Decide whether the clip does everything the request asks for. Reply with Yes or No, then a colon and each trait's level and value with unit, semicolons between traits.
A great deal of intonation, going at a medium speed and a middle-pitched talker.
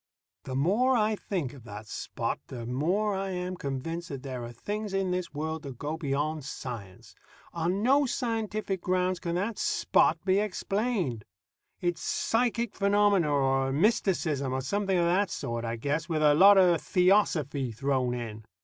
Yes: wide, 6.6 semitones; average, 165 wpm; medium, 170 Hz